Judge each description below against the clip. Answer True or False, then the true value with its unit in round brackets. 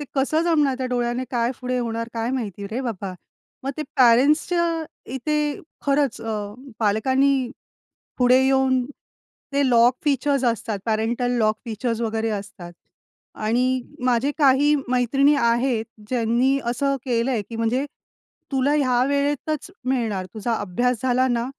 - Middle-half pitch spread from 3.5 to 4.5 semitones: False (2.9 semitones)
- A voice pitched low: False (250 Hz)